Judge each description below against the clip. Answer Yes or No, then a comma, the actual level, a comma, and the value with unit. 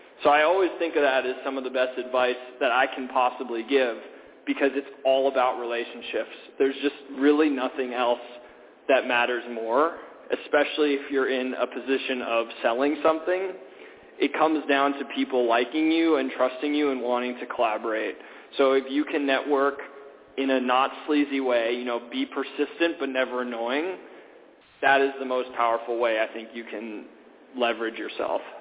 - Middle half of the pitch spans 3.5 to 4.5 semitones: No, narrow, 2.5 semitones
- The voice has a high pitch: No, low, 135 Hz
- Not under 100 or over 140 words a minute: No, average, 170 wpm